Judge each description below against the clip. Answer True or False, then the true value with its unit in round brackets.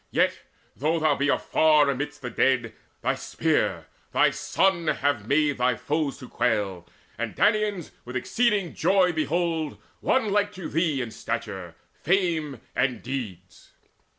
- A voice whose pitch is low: False (150 Hz)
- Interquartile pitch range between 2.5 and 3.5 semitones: False (5.4 semitones)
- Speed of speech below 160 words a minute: True (140 wpm)